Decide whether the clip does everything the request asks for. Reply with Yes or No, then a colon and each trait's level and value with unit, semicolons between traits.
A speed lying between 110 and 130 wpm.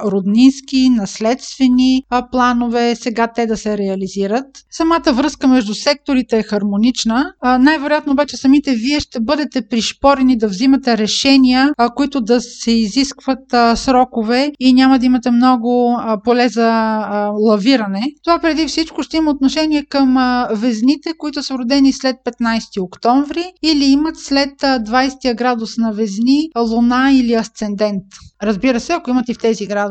No: average, 155 wpm